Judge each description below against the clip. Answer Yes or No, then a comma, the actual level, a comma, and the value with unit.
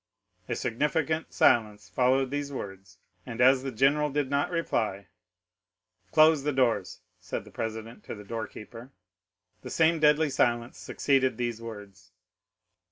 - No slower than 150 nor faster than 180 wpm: No, average, 140 wpm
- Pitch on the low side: Yes, low, 120 Hz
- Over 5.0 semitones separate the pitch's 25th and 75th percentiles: Yes, wide, 5.5 semitones